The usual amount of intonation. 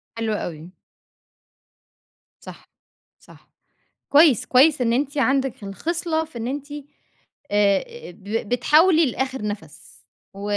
No: wide, 6.4 semitones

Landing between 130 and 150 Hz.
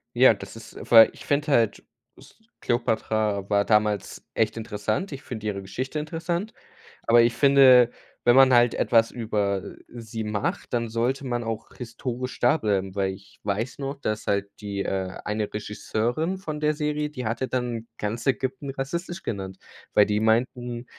No: low, 115 Hz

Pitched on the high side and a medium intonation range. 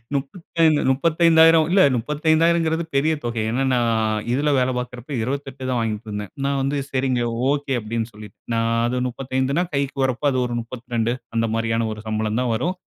No: low, 130 Hz; average, 4.5 semitones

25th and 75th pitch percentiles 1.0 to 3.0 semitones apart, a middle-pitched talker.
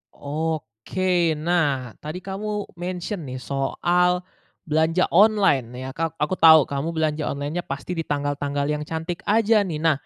No: average, 3.8 semitones; medium, 160 Hz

